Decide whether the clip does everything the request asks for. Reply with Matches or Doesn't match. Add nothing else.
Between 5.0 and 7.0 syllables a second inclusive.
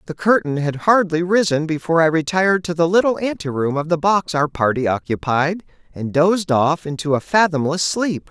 Matches